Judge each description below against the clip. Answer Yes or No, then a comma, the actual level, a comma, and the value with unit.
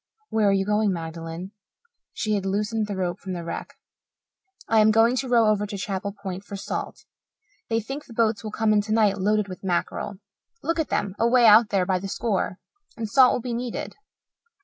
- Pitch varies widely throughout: No, average, 2.7 semitones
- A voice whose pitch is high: Yes, high, 210 Hz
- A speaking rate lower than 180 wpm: No, average, 200 wpm